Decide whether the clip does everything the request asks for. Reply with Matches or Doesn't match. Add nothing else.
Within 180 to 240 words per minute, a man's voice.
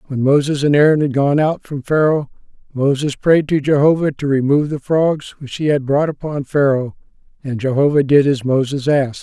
Matches